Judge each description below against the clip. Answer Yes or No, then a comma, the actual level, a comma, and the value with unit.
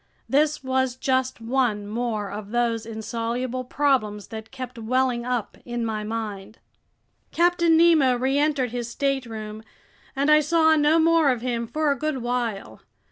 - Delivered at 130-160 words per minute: Yes, average, 145 wpm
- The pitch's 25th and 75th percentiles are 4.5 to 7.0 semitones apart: No, average, 3.7 semitones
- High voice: Yes, very high, 250 Hz